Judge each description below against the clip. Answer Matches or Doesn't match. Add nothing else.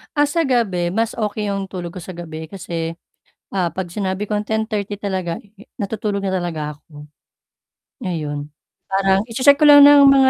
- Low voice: Doesn't match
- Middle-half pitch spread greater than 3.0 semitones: Matches